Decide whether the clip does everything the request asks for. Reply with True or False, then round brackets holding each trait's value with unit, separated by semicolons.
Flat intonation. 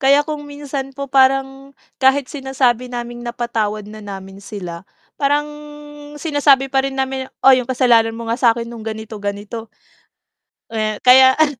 False (3.2 semitones)